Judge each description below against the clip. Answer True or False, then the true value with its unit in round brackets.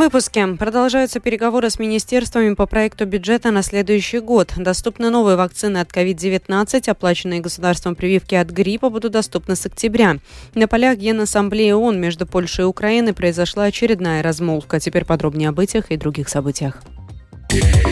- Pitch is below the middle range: False (200 Hz)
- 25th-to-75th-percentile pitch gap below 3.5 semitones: False (4.3 semitones)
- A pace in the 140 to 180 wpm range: True (145 wpm)